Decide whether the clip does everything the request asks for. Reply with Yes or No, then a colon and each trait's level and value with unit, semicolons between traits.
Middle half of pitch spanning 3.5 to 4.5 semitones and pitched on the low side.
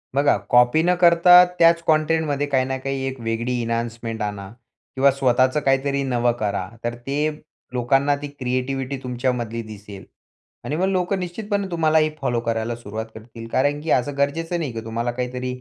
Yes: average, 4.0 semitones; low, 130 Hz